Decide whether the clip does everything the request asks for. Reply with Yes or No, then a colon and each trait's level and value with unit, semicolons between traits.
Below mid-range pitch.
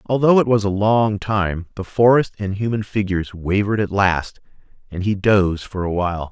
Yes: low, 100 Hz